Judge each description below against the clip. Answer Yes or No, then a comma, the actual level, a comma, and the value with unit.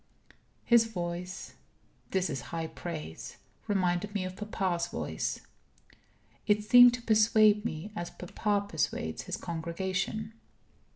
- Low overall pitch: No, high, 195 Hz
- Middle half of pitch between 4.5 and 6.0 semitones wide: No, average, 3.6 semitones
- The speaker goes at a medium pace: No, slow, 115 wpm